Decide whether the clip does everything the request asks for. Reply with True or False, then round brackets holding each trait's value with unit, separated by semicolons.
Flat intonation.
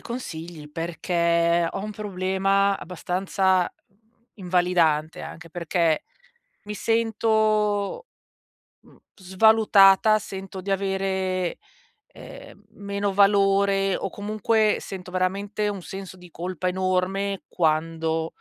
True (2.2 semitones)